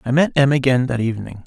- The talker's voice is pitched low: Yes, low, 130 Hz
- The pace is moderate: No, fast, 245 wpm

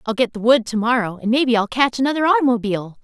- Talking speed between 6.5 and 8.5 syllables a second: Yes, 7.0 syllables/s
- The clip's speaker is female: Yes, female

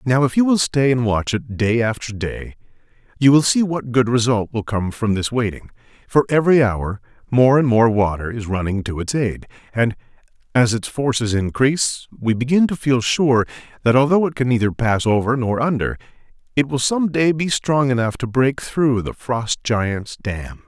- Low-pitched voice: Yes, low, 125 Hz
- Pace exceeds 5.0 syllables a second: No, 4.8 syllables/s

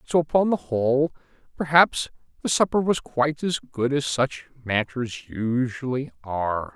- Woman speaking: No, male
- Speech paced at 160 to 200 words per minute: No, average, 140 wpm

